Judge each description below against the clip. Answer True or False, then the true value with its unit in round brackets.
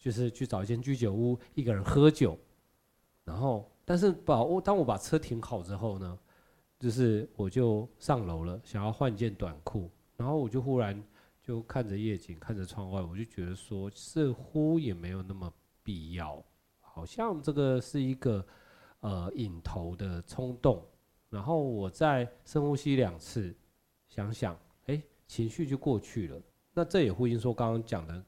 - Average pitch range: False (5.8 semitones)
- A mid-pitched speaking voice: False (115 Hz)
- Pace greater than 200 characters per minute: True (240 characters per minute)